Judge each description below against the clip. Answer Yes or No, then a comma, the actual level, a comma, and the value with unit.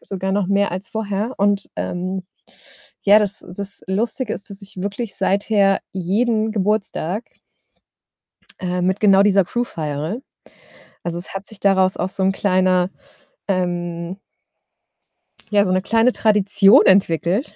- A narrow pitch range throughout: Yes, narrow, 2.0 semitones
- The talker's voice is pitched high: Yes, high, 195 Hz